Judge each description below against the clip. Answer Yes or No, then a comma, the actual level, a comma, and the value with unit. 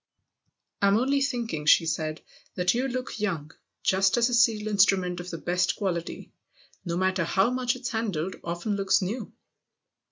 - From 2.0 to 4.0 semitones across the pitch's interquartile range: No, average, 5.0 semitones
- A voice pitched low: No, high, 195 Hz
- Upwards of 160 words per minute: Yes, average, 170 wpm